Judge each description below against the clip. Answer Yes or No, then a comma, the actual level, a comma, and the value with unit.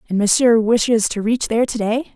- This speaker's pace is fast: Yes, fast, 220 wpm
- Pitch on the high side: Yes, high, 225 Hz